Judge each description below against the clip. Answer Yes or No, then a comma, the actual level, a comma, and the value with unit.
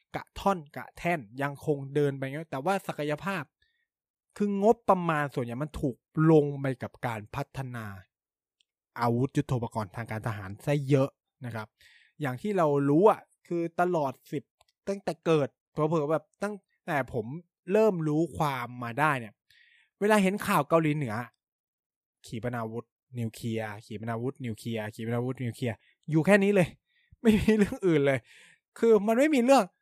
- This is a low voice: No, medium, 145 Hz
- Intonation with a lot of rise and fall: Yes, wide, 7.1 semitones